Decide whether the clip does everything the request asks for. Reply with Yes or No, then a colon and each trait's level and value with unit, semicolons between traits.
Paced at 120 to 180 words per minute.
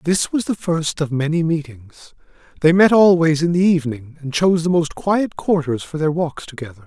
No: average, 200 wpm